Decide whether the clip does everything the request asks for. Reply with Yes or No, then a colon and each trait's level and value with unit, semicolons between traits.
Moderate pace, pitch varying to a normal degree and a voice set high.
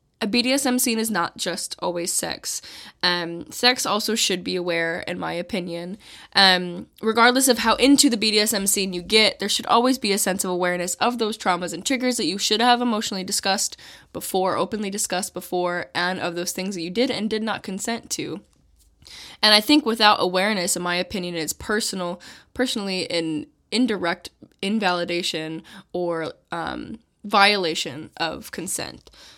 Yes: average, 165 wpm; average, 4.0 semitones; high, 195 Hz